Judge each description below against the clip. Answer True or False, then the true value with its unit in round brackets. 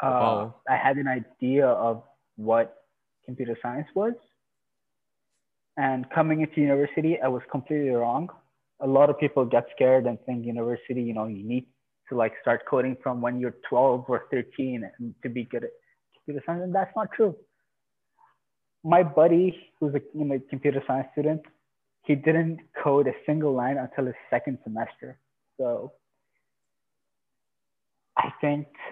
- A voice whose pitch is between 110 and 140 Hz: True (135 Hz)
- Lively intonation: False (3.7 semitones)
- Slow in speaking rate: False (155 wpm)